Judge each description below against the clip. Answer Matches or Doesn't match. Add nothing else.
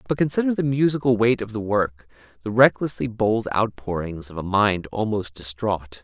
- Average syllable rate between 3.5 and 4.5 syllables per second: Doesn't match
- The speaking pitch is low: Matches